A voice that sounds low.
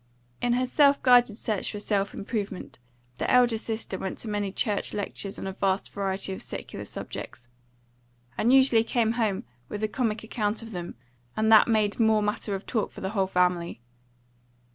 No: high, 210 Hz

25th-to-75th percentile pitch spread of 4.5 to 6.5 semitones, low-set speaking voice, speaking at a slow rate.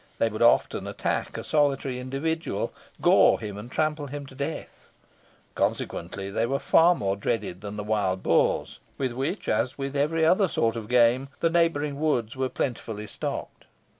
No: average, 5.1 semitones; low, 130 Hz; average, 165 wpm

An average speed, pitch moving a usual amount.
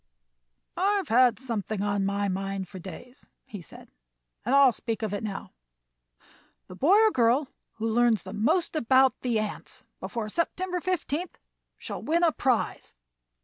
No: average, 145 wpm; wide, 6.6 semitones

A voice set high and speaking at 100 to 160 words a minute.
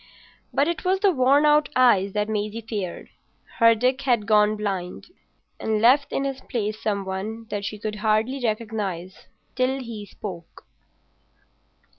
Yes: high, 220 Hz; average, 150 wpm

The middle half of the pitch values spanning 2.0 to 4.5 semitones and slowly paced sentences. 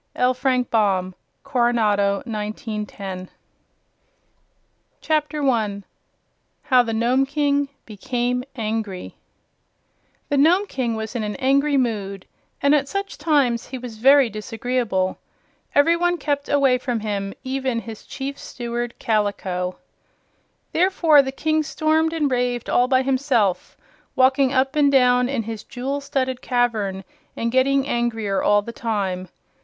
Yes: average, 4.2 semitones; slow, 130 wpm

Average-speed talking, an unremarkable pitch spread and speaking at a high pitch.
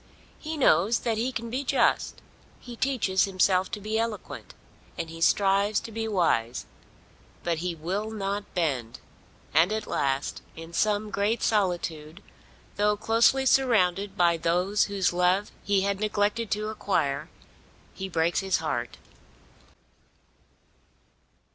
No: slow, 130 wpm; average, 4.0 semitones; high, 200 Hz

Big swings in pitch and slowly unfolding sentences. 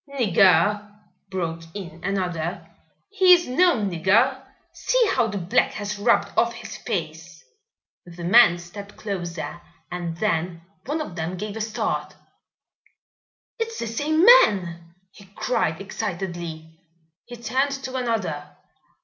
Yes: wide, 5.9 semitones; slow, 125 wpm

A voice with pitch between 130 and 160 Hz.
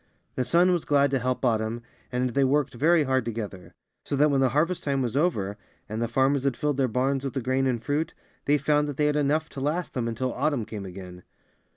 Yes: low, 135 Hz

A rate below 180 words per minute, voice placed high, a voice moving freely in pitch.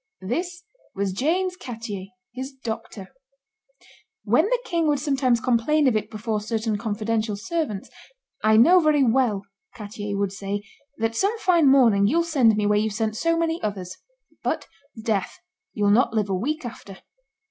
Yes: average, 160 wpm; high, 230 Hz; wide, 6.1 semitones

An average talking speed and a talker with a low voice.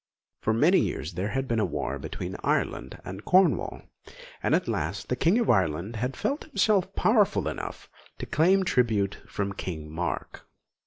Yes: average, 160 wpm; low, 115 Hz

